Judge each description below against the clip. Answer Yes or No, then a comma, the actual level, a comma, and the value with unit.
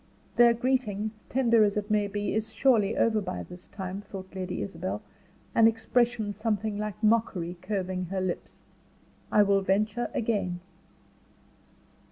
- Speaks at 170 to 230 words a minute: No, average, 140 wpm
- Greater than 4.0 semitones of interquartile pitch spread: No, average, 2.9 semitones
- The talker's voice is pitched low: No, high, 210 Hz